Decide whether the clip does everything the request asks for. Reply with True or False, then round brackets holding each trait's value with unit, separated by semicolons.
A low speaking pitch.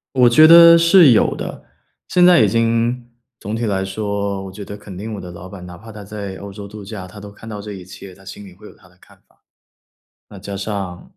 True (100 Hz)